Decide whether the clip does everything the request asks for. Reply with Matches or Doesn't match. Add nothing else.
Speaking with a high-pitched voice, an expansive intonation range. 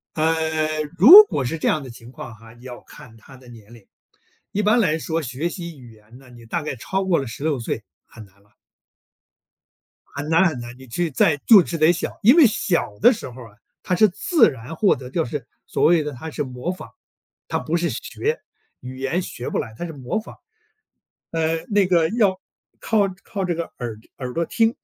Doesn't match